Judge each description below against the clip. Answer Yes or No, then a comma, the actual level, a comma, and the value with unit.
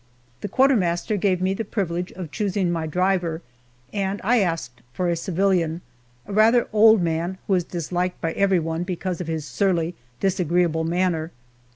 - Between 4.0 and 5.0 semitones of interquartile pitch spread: No, average, 2.8 semitones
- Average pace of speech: Yes, average, 160 wpm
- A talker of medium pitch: Yes, medium, 180 Hz